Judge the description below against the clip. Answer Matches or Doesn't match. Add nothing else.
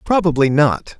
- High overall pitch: Doesn't match